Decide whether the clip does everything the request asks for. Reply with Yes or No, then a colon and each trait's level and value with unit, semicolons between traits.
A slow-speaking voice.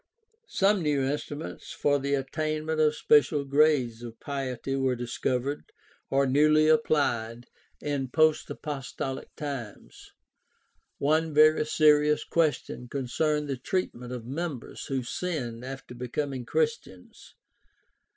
Yes: slow, 110 wpm